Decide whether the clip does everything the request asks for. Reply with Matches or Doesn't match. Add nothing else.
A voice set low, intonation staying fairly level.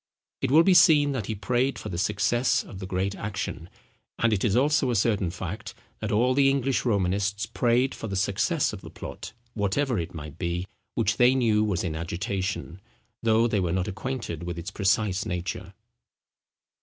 Doesn't match